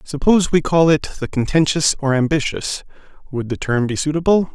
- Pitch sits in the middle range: Yes, medium, 150 Hz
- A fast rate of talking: No, average, 160 wpm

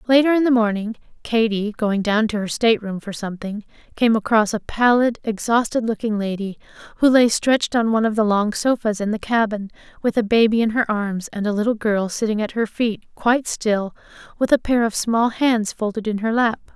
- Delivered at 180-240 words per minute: Yes, fast, 205 wpm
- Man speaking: No, female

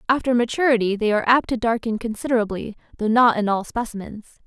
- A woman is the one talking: Yes, female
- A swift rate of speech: No, average, 175 wpm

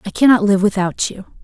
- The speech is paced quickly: Yes, fast, 210 wpm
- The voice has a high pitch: Yes, high, 200 Hz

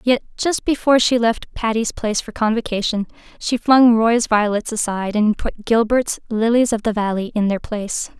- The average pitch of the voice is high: Yes, high, 225 Hz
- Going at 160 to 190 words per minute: Yes, average, 175 wpm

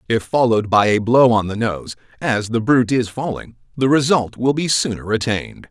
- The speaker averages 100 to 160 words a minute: No, average, 200 wpm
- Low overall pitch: Yes, low, 120 Hz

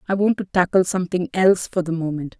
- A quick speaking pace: Yes, fast, 225 wpm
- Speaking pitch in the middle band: Yes, medium, 180 Hz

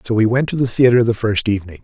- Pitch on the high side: No, low, 115 Hz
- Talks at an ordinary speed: No, fast, 295 wpm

